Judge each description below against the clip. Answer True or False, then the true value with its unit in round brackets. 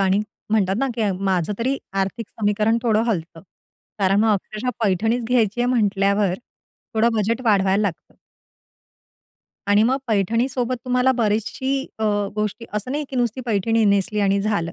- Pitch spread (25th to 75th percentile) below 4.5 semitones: True (2.9 semitones)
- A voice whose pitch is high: True (215 Hz)